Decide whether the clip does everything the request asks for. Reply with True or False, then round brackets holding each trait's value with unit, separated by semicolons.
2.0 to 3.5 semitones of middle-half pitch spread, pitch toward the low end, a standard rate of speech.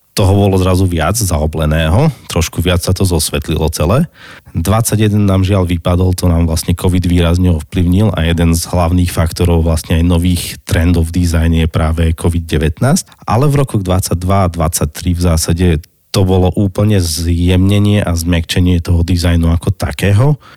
True (2.5 semitones; 90 Hz; 155 wpm)